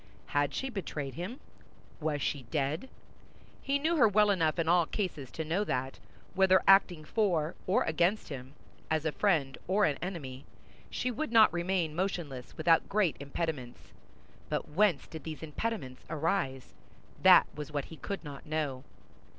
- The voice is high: No, medium, 160 Hz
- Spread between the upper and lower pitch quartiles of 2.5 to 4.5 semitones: No, average, 5.0 semitones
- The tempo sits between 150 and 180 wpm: Yes, average, 160 wpm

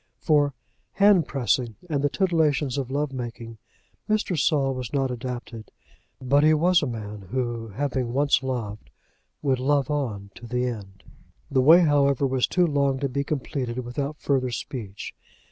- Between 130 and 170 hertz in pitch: Yes, low, 135 Hz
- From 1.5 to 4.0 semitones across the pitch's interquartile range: Yes, average, 3.2 semitones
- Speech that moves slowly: No, average, 160 wpm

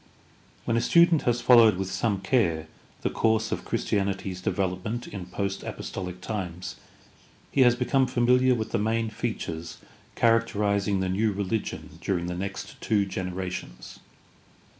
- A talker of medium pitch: No, low, 100 Hz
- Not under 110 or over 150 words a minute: Yes, average, 145 wpm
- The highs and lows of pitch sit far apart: No, average, 3.7 semitones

